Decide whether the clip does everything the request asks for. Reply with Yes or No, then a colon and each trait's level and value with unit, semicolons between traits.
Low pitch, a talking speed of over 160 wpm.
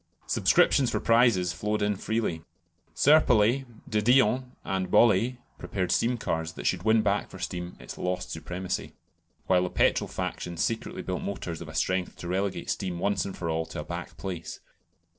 Yes: very low, 95 Hz; average, 175 wpm